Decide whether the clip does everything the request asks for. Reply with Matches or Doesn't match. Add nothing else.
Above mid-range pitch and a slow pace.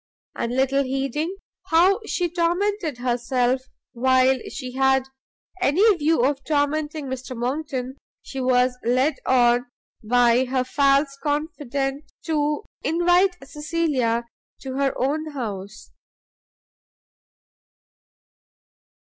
Matches